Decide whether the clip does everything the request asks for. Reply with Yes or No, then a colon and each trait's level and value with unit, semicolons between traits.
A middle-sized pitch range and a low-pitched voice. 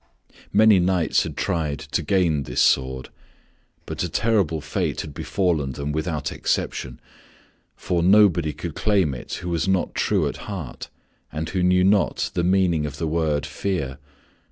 Yes: average, 4.1 semitones; very low, 85 Hz